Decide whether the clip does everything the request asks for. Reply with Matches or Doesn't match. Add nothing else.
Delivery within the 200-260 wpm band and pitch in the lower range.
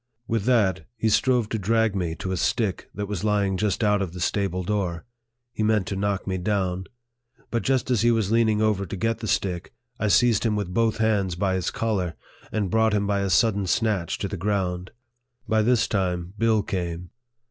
Matches